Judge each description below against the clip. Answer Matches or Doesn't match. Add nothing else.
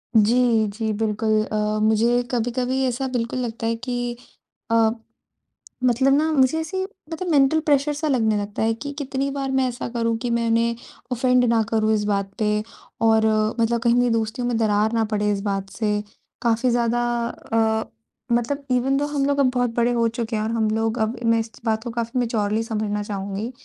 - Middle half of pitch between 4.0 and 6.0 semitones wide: Doesn't match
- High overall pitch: Matches